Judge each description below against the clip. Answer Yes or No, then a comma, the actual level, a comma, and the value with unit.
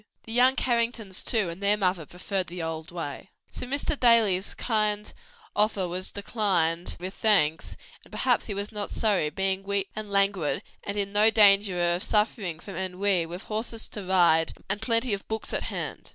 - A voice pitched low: No, high, 200 Hz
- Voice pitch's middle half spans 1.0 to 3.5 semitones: Yes, average, 3.1 semitones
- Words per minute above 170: Yes, average, 180 wpm